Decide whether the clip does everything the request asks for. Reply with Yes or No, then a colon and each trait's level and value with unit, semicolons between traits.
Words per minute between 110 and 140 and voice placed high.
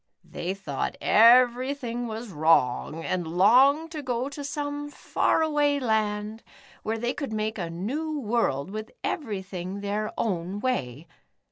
Yes: slow, 135 wpm; high, 220 Hz